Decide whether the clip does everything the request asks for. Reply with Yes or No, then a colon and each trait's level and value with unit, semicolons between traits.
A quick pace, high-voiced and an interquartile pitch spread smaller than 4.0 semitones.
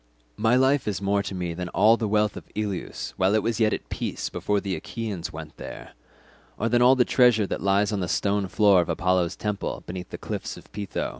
No: fast, 225 wpm; low, 100 Hz; average, 2.8 semitones